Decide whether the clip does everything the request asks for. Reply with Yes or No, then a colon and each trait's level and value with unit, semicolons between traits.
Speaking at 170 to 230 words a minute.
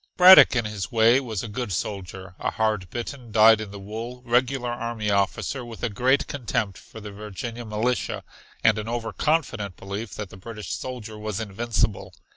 Yes: average, 180 wpm